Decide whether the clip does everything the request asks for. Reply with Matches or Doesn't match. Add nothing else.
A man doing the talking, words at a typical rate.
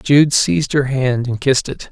Doesn't match